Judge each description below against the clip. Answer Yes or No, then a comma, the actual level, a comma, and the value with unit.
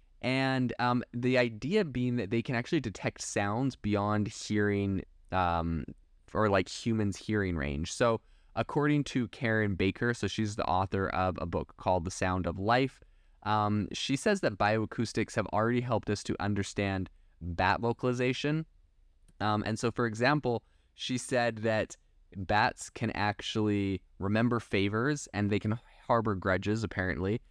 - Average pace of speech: Yes, average, 150 wpm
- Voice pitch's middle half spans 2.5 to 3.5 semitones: No, average, 4.0 semitones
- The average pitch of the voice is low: Yes, low, 105 Hz